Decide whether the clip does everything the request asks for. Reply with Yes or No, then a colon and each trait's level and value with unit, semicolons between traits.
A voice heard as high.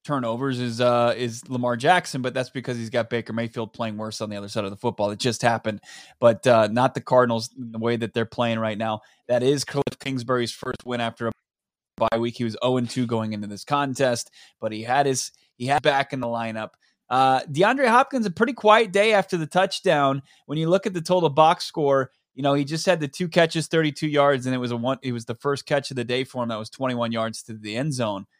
No: low, 125 Hz